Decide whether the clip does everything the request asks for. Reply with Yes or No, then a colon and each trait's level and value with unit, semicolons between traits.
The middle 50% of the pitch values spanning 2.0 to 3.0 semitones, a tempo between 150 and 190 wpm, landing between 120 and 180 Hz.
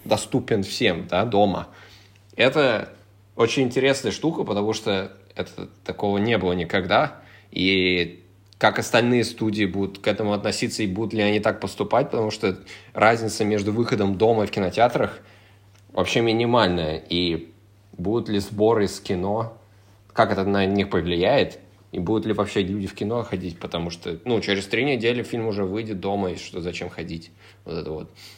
No: narrow, 2.6 semitones; fast, 160 wpm; low, 100 Hz